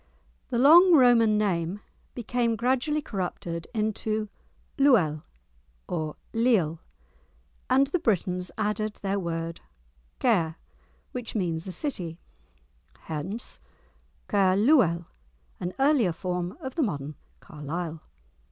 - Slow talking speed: Yes, slow, 100 wpm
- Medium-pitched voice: No, high, 200 Hz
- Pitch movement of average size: No, wide, 6.3 semitones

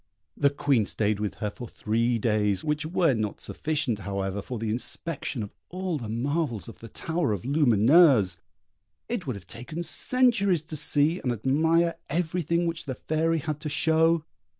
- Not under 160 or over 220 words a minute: Yes, average, 170 wpm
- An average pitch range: No, wide, 6.7 semitones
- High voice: No, medium, 145 Hz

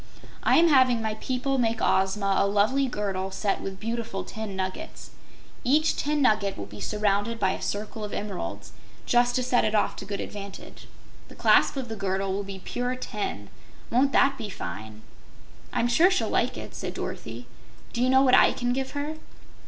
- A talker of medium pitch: No, high, 220 Hz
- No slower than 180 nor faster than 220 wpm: Yes, average, 190 wpm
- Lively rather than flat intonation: No, average, 4.4 semitones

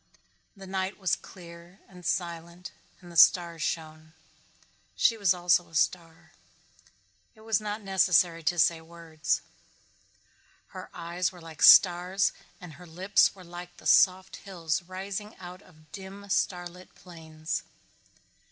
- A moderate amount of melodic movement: No, narrow, 2.2 semitones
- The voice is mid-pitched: Yes, medium, 175 Hz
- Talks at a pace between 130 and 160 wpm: Yes, slow, 135 wpm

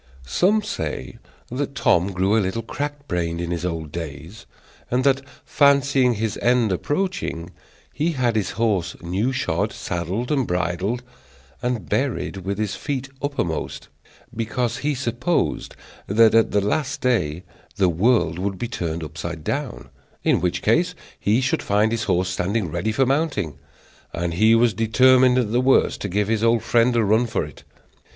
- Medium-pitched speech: No, low, 110 Hz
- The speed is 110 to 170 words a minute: Yes, average, 165 wpm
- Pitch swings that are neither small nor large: No, wide, 6.1 semitones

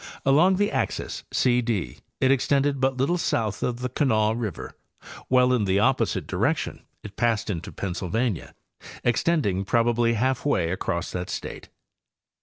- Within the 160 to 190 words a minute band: No, average, 145 wpm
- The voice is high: No, low, 120 Hz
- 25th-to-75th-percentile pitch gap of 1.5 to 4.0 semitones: No, average, 4.5 semitones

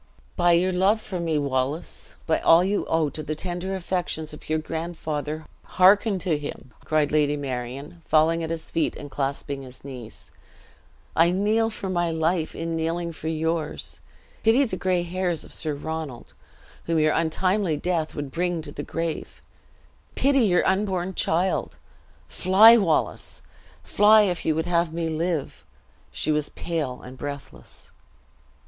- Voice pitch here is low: No, medium, 165 Hz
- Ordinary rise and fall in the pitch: Yes, average, 3.0 semitones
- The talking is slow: No, average, 155 wpm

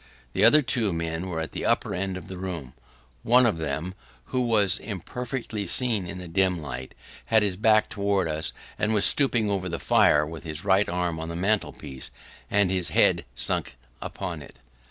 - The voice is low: Yes, very low, 95 Hz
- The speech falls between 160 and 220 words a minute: Yes, average, 195 wpm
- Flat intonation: No, average, 4.2 semitones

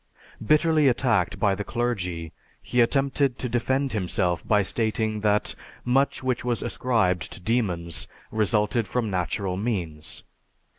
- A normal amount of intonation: Yes, average, 4.9 semitones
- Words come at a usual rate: No, slow, 130 wpm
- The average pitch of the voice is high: No, low, 110 Hz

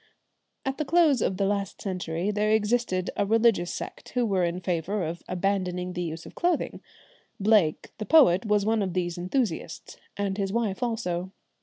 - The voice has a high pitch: Yes, high, 195 Hz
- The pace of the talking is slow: No, average, 175 wpm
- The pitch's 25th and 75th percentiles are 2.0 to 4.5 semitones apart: Yes, average, 3.7 semitones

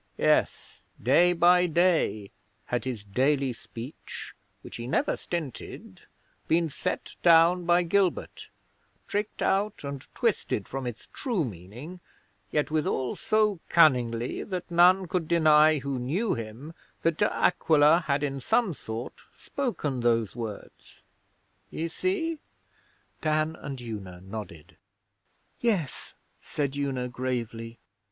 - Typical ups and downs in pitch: No, wide, 6.2 semitones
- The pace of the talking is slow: Yes, slow, 120 wpm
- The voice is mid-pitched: Yes, medium, 150 Hz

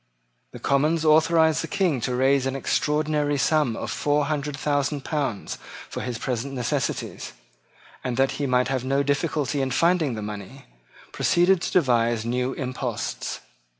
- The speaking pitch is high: No, medium, 140 Hz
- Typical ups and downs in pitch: Yes, average, 3.3 semitones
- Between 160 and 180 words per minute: No, average, 150 wpm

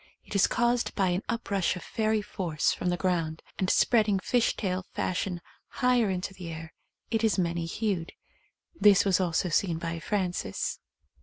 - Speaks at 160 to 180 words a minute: Yes, average, 175 wpm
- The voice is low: No, medium, 185 Hz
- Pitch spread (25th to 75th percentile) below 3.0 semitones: No, average, 3.7 semitones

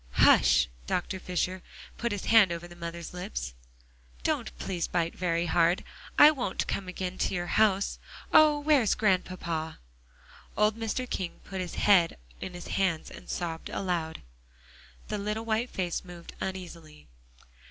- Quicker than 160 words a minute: No, average, 155 wpm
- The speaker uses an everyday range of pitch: Yes, average, 3.4 semitones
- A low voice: No, medium, 180 Hz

